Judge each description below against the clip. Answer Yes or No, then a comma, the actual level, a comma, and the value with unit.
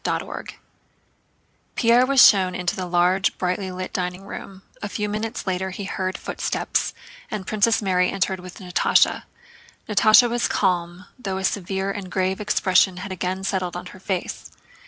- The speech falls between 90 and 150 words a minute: No, average, 160 wpm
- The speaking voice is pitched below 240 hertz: Yes, high, 190 Hz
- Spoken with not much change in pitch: Yes, narrow, 2.0 semitones